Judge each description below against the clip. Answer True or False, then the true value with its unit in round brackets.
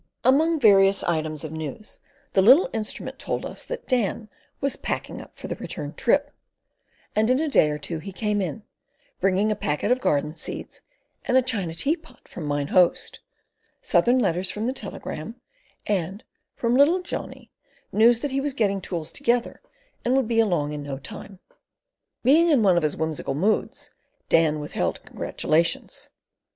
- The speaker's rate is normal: True (165 wpm)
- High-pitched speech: True (205 Hz)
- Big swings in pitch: True (7.6 semitones)